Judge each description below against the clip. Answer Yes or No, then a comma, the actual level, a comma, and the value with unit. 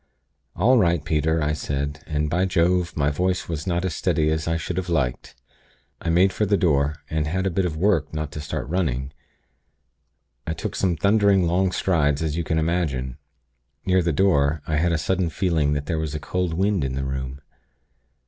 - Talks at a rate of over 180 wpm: Yes, average, 200 wpm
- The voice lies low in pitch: Yes, very low, 80 Hz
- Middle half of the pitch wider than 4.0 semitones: No, average, 3.5 semitones